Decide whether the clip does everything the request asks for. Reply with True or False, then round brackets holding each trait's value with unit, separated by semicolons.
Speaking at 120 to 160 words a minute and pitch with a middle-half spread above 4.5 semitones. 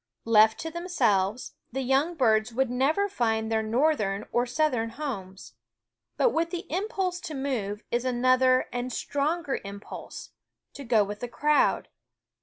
True (145 wpm; 5.6 semitones)